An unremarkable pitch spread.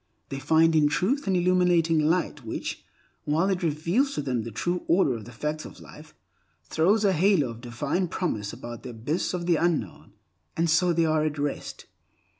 Yes: average, 4.4 semitones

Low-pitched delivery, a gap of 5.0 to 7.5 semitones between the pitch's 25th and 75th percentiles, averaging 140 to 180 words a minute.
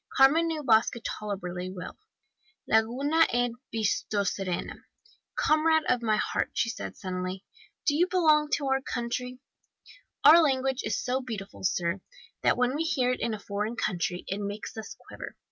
No: high, 235 Hz; wide, 5.4 semitones; average, 155 wpm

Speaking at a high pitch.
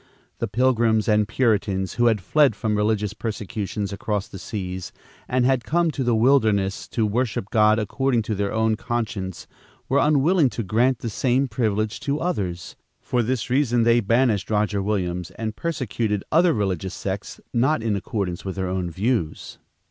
No: low, 110 Hz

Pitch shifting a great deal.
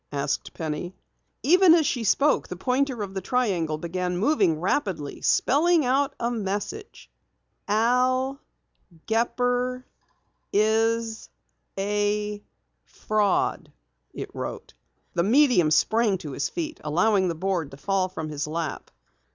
Yes: wide, 5.9 semitones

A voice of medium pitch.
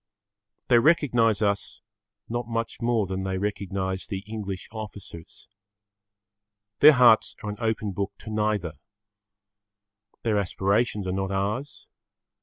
No: low, 105 Hz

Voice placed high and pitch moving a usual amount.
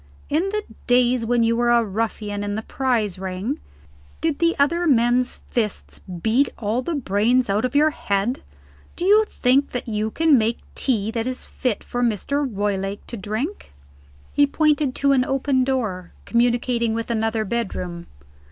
Yes: high, 240 Hz; average, 4.2 semitones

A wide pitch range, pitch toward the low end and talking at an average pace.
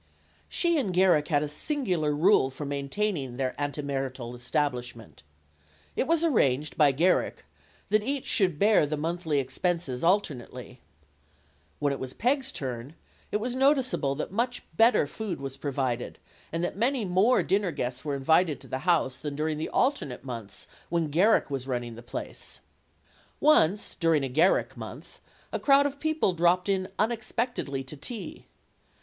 No: wide, 7.5 semitones; medium, 160 Hz; average, 155 wpm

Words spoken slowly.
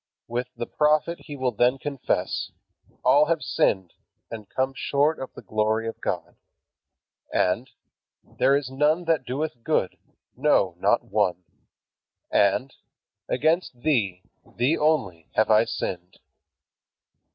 Yes: slow, 125 wpm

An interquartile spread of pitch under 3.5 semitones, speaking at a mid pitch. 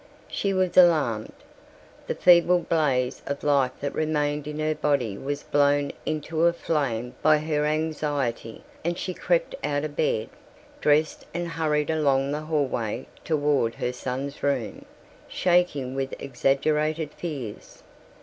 Yes: narrow, 2.6 semitones; medium, 150 Hz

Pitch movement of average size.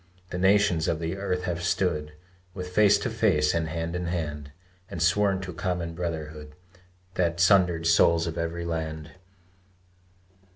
No: narrow, 2.0 semitones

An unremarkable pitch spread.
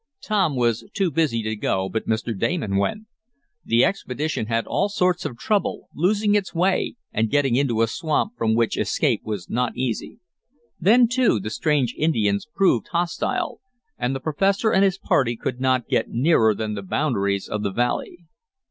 No: wide, 8.4 semitones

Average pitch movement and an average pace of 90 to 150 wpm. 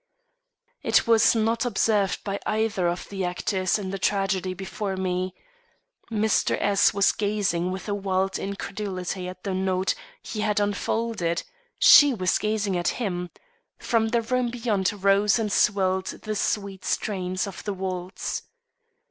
No: narrow, 2.3 semitones; average, 145 wpm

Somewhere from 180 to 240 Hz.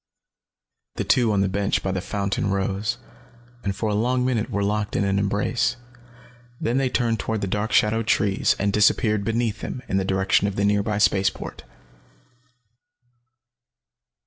No: low, 105 Hz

